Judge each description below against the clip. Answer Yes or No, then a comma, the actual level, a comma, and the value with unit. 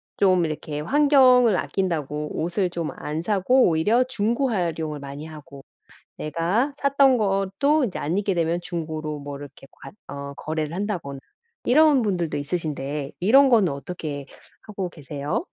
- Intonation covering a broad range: Yes, wide, 6.3 semitones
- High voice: No, medium, 170 Hz